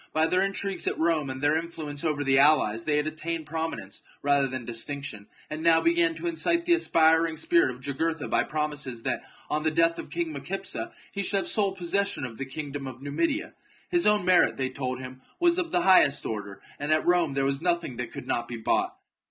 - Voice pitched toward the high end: No, medium, 155 Hz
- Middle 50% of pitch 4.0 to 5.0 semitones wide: Yes, average, 4.6 semitones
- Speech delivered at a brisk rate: Yes, fast, 215 wpm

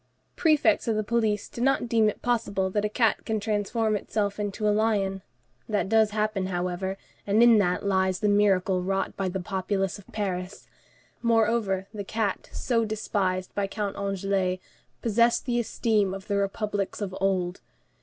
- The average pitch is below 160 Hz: No, high, 205 Hz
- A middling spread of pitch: No, narrow, 2.3 semitones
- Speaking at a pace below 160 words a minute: No, average, 165 wpm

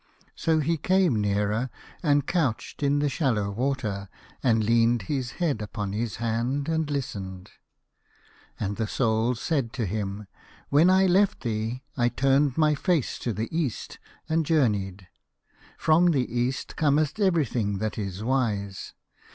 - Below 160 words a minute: Yes, average, 150 wpm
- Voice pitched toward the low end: Yes, low, 125 Hz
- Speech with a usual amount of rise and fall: No, wide, 5.7 semitones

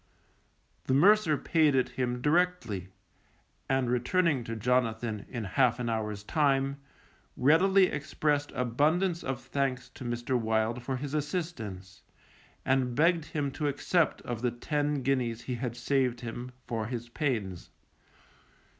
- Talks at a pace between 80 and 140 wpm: Yes, slow, 135 wpm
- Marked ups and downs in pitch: No, average, 3.8 semitones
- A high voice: No, low, 130 Hz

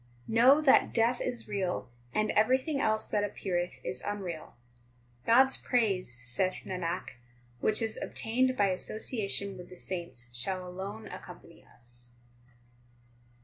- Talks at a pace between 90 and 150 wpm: Yes, average, 140 wpm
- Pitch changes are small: No, average, 4.2 semitones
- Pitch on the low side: No, high, 200 Hz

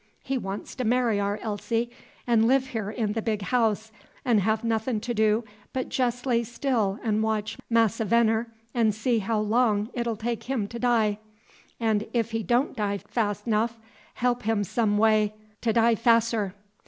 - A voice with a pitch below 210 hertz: No, high, 225 Hz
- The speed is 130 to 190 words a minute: Yes, average, 180 wpm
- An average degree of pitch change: No, narrow, 1.9 semitones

